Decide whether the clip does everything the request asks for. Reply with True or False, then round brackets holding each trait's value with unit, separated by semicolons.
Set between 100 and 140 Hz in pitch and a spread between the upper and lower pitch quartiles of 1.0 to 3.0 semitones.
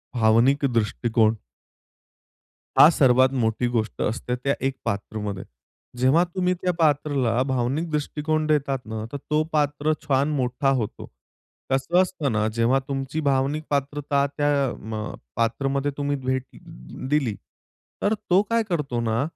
False (135 Hz; 4.0 semitones)